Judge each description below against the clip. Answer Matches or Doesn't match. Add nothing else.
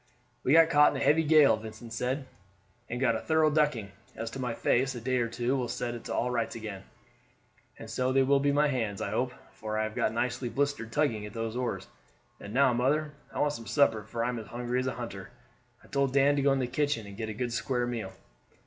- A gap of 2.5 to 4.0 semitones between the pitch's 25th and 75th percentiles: Matches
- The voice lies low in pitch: Matches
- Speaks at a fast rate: Matches